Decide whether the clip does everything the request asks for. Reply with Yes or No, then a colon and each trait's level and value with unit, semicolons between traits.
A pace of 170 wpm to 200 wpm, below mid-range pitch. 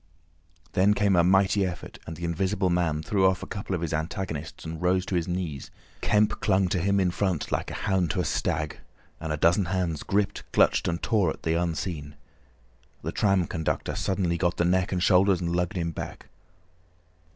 Yes: average, 195 wpm; very low, 90 Hz